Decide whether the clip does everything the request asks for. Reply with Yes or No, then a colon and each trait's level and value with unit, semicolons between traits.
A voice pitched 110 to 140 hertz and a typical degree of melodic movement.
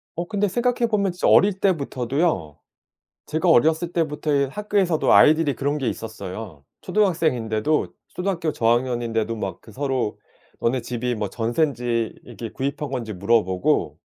No: low, 135 Hz; wide, 6.6 semitones